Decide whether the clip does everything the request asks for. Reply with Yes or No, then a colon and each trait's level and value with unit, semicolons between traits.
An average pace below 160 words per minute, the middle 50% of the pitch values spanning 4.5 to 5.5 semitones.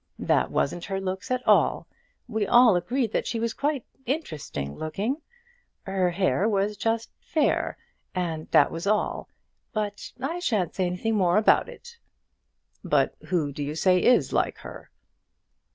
Yes: average, 150 wpm; average, 5.1 semitones